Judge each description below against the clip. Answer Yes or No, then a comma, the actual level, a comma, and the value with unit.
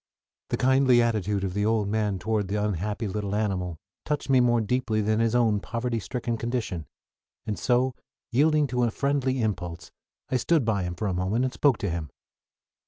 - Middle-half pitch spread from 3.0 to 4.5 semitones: Yes, average, 3.7 semitones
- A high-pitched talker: No, low, 110 Hz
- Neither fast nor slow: Yes, average, 185 wpm